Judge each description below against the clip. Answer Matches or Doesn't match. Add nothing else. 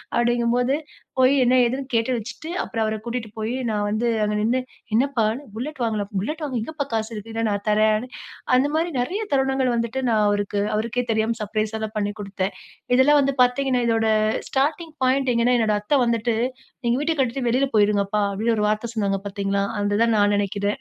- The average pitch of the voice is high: Matches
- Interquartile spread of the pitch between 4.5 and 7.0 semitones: Doesn't match